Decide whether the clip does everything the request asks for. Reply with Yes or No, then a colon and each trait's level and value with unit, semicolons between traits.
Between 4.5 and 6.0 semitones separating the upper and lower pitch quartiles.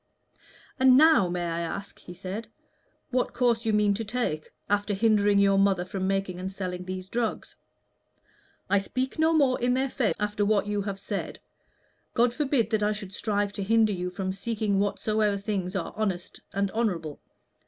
No: average, 2.9 semitones